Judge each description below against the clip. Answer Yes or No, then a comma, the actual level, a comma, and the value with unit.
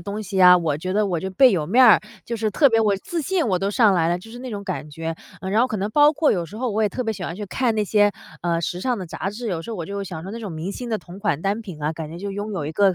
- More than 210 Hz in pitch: No, high, 200 Hz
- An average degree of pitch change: Yes, average, 4.1 semitones